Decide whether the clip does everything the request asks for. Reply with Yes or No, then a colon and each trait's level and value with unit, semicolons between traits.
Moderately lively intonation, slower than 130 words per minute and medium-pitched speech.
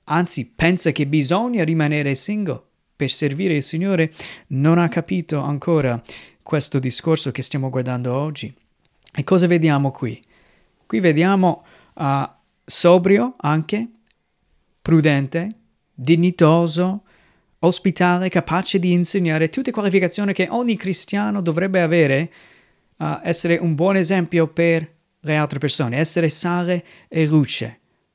Yes: average, 3.5 semitones; average, 120 wpm; medium, 165 Hz